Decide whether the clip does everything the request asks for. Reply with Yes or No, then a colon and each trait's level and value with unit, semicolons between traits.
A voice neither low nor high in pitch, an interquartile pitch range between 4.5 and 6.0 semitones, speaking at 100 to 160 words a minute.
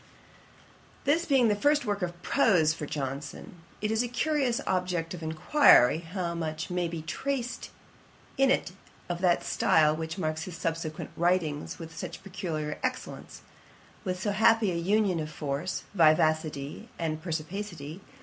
Yes: medium, 170 Hz; average, 4.9 semitones; average, 145 wpm